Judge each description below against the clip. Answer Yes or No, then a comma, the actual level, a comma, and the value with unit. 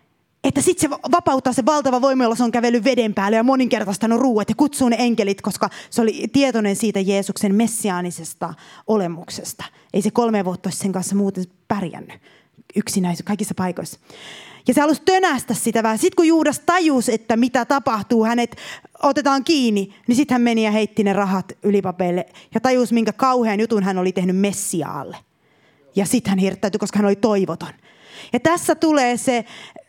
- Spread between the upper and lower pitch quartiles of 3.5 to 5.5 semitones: Yes, average, 4.5 semitones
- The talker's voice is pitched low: No, high, 225 Hz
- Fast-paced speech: Yes, fast, 170 wpm